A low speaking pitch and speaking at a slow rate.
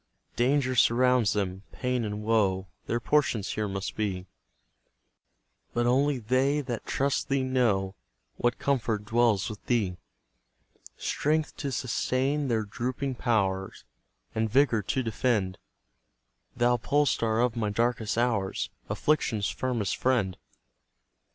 Yes: low, 120 Hz; slow, 120 wpm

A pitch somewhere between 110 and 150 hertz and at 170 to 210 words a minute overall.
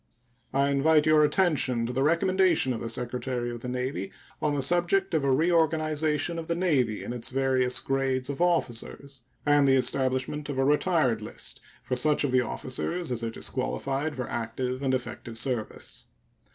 Yes: low, 135 Hz; average, 175 wpm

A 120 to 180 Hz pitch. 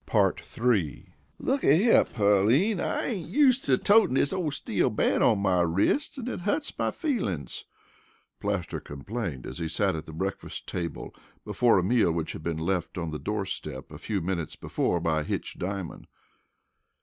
No: low, 100 Hz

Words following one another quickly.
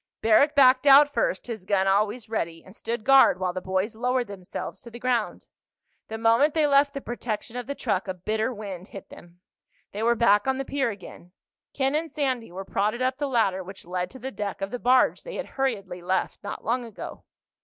Yes: fast, 215 wpm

